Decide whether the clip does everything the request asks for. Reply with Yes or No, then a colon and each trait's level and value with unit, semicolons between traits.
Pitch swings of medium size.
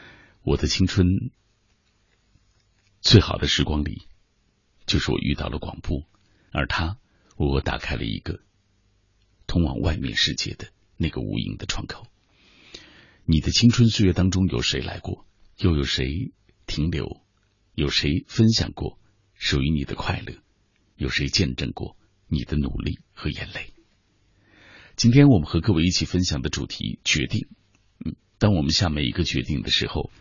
Yes: average, 4.5 semitones